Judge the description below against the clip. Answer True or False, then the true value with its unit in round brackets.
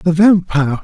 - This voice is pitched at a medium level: True (170 Hz)